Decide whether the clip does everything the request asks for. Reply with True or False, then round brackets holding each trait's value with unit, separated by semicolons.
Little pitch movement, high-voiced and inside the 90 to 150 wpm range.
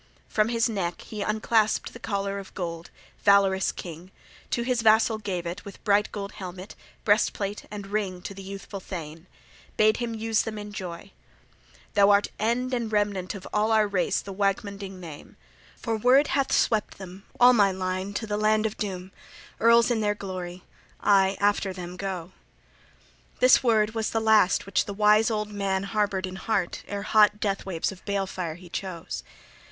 False (2.2 semitones; 200 Hz; 175 wpm)